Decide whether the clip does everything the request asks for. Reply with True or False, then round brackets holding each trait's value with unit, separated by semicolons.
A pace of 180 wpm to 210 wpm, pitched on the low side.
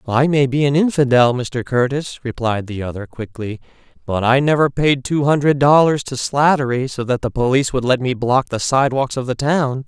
True (200 wpm; 130 Hz)